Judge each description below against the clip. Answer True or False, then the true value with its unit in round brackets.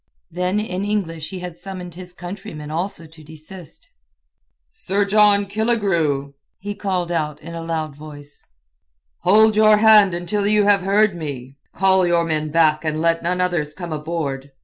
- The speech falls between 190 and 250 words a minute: False (155 wpm)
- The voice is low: False (175 Hz)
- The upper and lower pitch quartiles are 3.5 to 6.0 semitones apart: True (4.3 semitones)